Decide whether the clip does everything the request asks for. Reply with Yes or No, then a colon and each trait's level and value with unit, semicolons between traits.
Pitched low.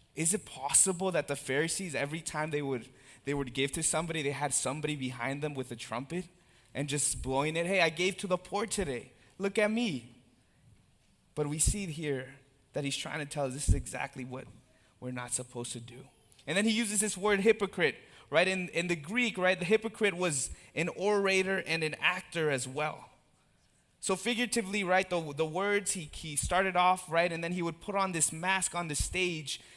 No: medium, 160 Hz